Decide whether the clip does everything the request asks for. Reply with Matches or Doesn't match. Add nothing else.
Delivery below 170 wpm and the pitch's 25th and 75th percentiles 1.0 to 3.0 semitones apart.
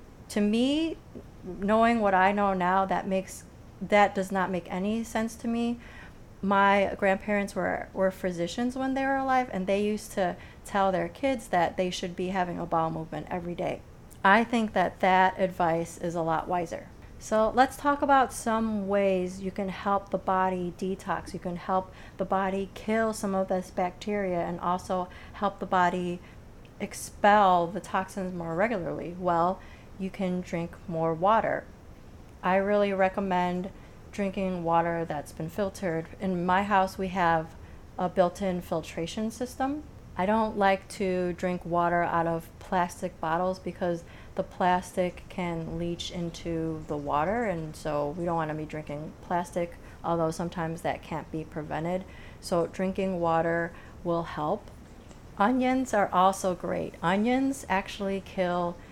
Matches